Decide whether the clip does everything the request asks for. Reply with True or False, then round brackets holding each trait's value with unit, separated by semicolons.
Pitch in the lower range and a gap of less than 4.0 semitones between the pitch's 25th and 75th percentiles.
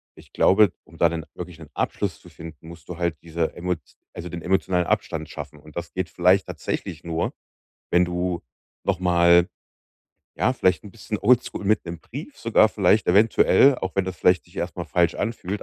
True (90 Hz; 2.4 semitones)